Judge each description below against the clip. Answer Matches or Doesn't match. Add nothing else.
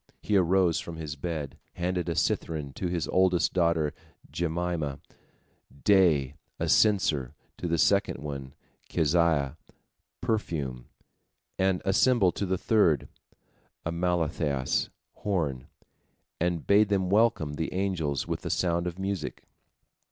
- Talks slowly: Matches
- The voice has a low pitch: Matches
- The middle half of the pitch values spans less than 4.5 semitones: Matches